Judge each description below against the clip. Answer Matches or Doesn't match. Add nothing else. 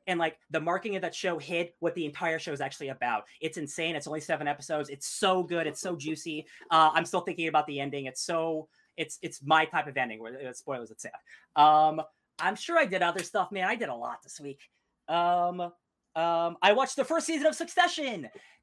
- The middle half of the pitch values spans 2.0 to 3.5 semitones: Matches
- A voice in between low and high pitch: Matches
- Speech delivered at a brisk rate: Matches